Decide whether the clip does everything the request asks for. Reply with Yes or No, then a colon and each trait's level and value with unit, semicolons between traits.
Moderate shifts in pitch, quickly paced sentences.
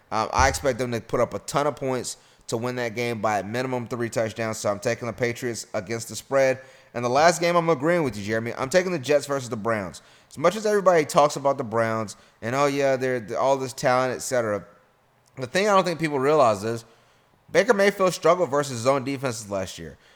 Yes: average, 3.7 semitones; fast, 235 wpm